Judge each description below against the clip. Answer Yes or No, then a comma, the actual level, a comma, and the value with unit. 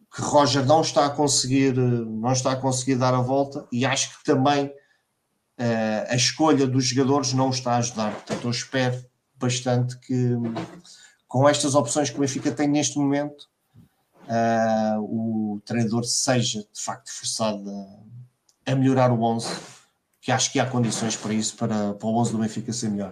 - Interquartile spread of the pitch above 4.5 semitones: No, average, 3.5 semitones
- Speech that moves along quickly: No, average, 175 wpm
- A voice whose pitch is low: Yes, low, 125 Hz